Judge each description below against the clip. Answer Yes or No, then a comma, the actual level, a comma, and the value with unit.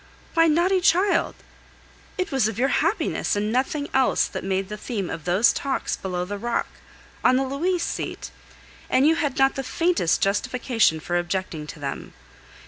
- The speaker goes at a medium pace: Yes, average, 170 wpm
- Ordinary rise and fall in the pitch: No, wide, 7.8 semitones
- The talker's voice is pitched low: No, very high, 250 Hz